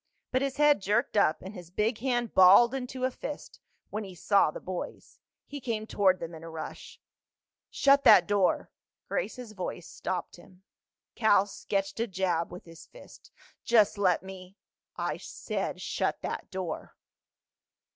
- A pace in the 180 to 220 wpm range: No, average, 155 wpm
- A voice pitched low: No, high, 200 Hz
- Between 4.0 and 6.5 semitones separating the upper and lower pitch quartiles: Yes, average, 4.6 semitones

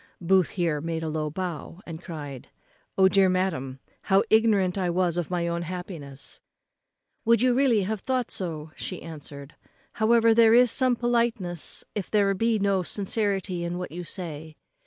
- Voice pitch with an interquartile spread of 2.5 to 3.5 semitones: No, average, 4.7 semitones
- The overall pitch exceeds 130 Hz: Yes, medium, 185 Hz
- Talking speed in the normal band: Yes, average, 165 wpm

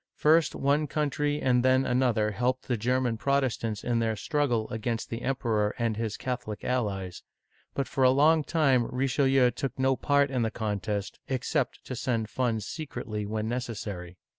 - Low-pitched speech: Yes, low, 125 Hz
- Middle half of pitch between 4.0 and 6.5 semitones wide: No, average, 3.5 semitones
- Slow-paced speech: No, average, 165 wpm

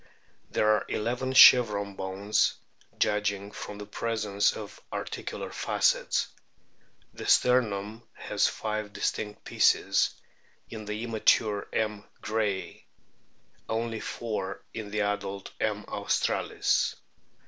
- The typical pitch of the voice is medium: No, low, 105 Hz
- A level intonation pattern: Yes, narrow, 1.5 semitones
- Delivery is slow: Yes, slow, 105 wpm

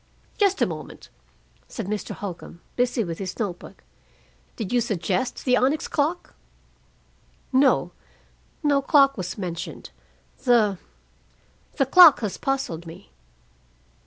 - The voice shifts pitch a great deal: Yes, wide, 6.7 semitones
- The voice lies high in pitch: Yes, high, 235 Hz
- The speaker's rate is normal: No, slow, 120 wpm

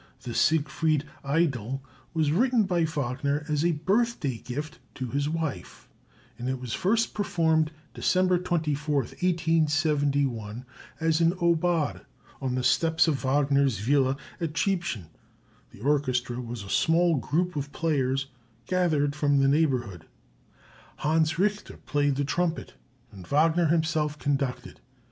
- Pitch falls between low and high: Yes, medium, 150 Hz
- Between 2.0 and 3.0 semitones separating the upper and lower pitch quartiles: No, average, 3.5 semitones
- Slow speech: Yes, slow, 130 wpm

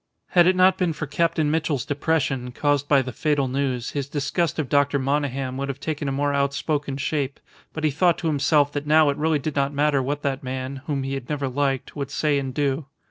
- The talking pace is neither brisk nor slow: No, fast, 225 wpm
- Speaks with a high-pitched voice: No, medium, 145 Hz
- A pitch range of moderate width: No, narrow, 1.9 semitones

